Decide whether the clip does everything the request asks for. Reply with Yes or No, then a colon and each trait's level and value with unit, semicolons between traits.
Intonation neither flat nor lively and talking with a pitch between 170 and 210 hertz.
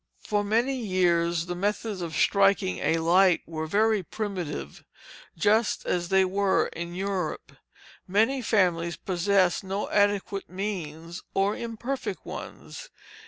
Yes: average, 3.2 semitones; high, 190 Hz